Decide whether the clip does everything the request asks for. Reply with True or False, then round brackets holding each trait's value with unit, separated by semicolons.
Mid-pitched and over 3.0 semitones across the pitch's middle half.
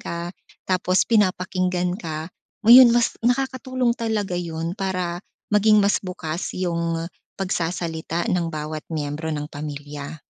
True (175 Hz; 3.8 semitones)